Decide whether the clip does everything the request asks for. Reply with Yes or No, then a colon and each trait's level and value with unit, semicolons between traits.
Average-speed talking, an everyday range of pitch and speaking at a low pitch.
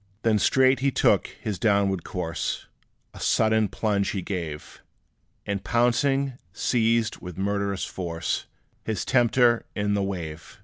No: slow, 130 wpm; average, 3.7 semitones; low, 105 Hz